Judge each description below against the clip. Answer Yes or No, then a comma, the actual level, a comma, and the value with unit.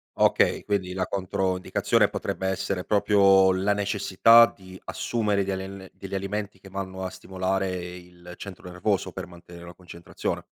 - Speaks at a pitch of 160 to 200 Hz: No, very low, 95 Hz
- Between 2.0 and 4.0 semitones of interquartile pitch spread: No, narrow, 1.3 semitones